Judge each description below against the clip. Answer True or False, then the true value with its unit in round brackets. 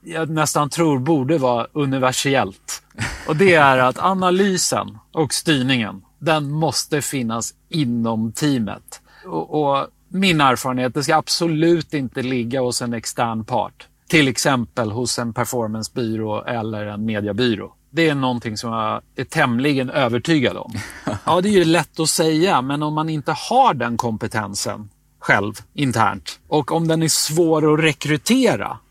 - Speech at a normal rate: True (150 wpm)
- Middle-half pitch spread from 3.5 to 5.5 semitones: True (5.1 semitones)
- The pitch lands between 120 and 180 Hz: True (135 Hz)